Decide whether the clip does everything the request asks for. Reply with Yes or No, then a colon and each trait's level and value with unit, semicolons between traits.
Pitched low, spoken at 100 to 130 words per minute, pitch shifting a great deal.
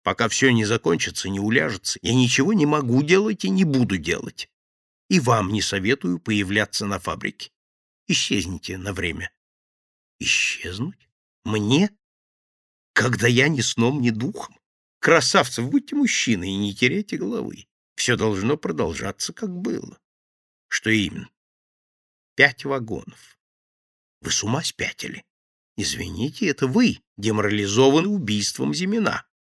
Yes: low, 115 Hz; average, 120 wpm; wide, 5.9 semitones